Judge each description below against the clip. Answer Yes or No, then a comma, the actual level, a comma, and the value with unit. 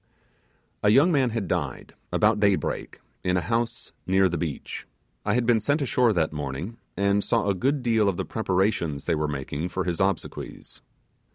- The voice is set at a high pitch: No, low, 100 Hz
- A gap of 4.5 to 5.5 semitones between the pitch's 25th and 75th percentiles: Yes, average, 4.8 semitones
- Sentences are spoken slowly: No, average, 180 wpm